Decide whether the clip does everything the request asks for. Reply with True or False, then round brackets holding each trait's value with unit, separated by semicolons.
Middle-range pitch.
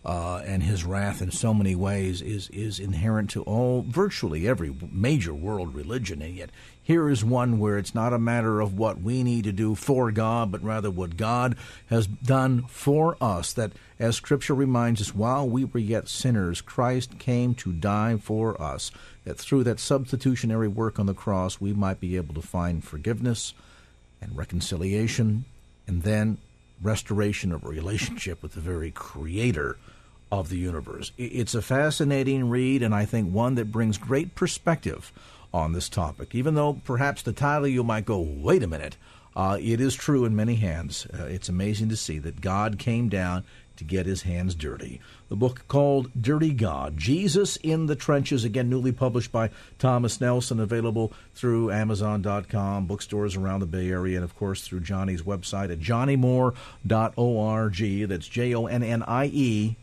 False (110 Hz)